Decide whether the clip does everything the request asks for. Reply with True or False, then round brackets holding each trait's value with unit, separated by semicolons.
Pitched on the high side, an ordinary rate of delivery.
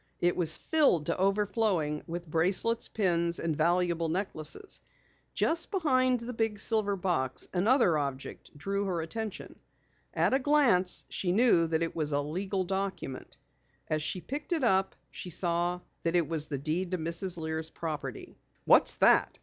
False (180 Hz; 160 wpm)